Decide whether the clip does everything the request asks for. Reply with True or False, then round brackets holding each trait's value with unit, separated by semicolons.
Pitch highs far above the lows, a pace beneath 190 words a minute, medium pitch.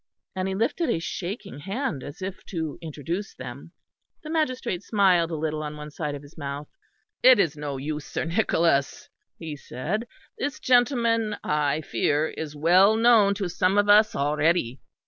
True (5.9 semitones; 165 wpm; 170 Hz)